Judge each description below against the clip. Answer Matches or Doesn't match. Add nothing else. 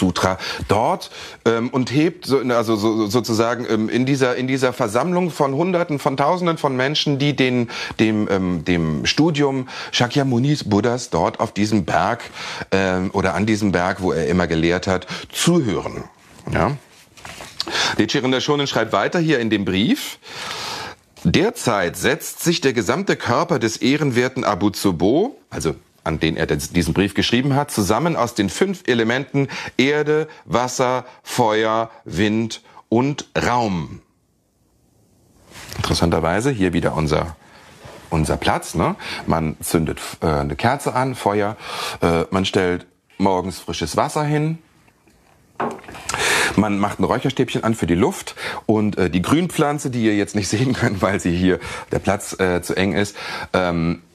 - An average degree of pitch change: Doesn't match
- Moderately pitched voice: Doesn't match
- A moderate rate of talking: Matches